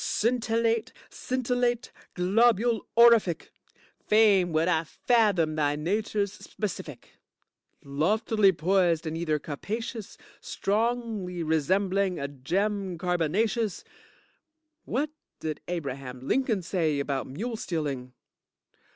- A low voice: No, high, 190 Hz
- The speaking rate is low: Yes, slow, 90 wpm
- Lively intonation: Yes, wide, 6.0 semitones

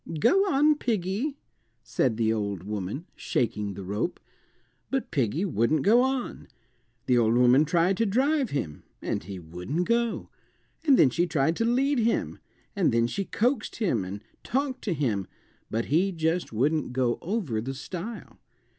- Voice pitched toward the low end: No, medium, 160 Hz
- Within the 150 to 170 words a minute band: Yes, average, 160 wpm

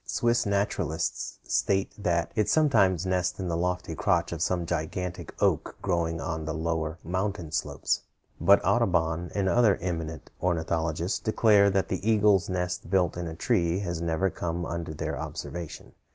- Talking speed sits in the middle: Yes, average, 155 wpm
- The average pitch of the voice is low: Yes, very low, 90 Hz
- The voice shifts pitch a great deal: No, average, 2.8 semitones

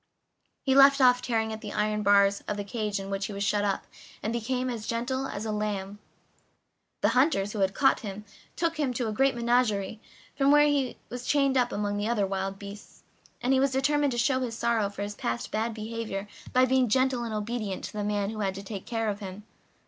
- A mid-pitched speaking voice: No, high, 220 Hz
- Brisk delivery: Yes, fast, 225 wpm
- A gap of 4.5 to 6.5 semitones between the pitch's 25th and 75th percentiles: No, average, 3.9 semitones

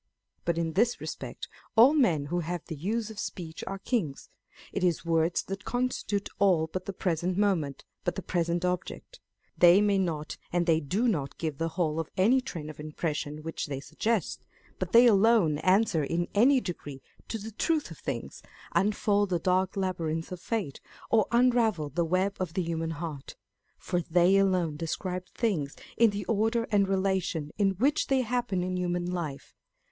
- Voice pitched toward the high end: No, medium, 180 Hz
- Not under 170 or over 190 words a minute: Yes, average, 180 wpm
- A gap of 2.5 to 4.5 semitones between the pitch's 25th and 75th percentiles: Yes, average, 4.0 semitones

